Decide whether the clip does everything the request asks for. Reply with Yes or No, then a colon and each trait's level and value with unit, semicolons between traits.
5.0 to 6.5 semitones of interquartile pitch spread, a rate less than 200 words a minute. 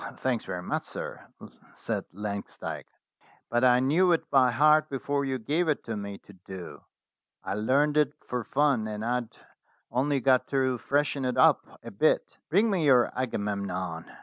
Yes: average, 5.3 semitones; average, 170 wpm